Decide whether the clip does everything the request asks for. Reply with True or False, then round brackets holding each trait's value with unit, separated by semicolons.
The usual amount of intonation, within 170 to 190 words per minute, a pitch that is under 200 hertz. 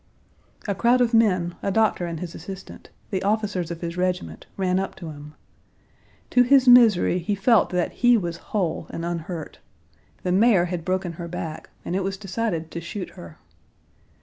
True (3.6 semitones; 175 wpm; 185 Hz)